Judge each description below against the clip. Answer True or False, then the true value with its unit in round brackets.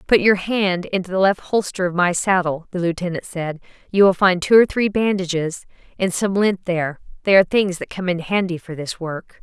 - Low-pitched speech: False (185 Hz)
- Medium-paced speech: False (215 wpm)